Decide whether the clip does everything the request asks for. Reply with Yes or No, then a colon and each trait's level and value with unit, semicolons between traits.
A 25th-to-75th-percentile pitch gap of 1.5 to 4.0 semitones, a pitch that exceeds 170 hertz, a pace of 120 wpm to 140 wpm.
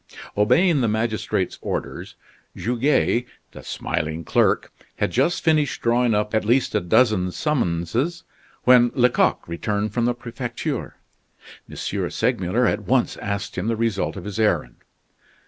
No: average, 3.4 semitones; low, 115 Hz; slow, 135 wpm